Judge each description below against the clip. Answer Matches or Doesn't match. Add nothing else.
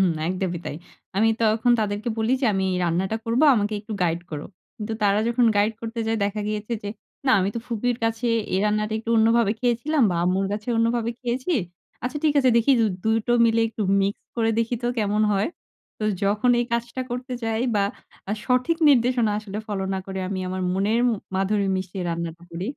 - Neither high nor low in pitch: Doesn't match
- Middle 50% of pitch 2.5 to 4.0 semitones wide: Matches